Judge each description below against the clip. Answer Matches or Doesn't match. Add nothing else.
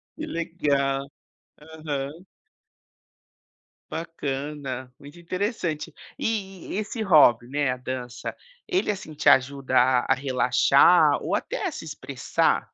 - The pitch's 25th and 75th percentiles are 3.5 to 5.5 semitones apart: Matches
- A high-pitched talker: Doesn't match